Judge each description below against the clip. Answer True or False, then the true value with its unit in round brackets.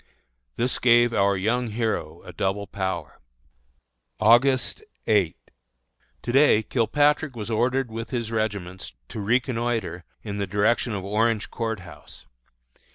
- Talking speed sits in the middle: False (125 wpm)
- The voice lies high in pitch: False (110 Hz)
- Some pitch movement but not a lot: True (3.2 semitones)